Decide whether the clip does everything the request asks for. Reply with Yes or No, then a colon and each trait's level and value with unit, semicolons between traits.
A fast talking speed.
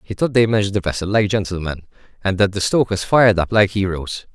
Yes: fast, 220 wpm